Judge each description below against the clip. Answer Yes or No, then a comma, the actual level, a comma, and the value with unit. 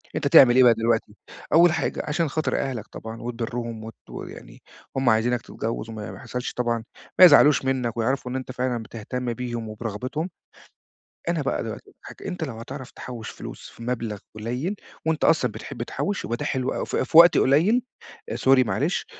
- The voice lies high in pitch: No, low, 125 Hz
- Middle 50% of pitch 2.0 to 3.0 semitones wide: No, average, 3.5 semitones